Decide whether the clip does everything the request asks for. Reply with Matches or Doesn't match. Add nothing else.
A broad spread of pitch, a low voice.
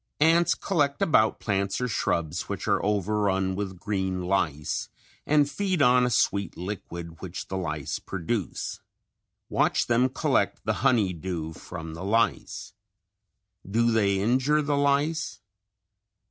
Matches